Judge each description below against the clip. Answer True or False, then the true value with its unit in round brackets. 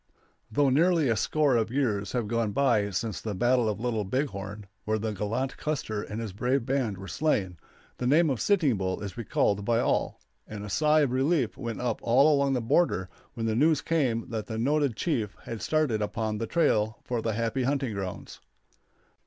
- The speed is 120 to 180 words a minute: False (205 wpm)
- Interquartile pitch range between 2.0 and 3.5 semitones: False (4.5 semitones)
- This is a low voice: True (115 Hz)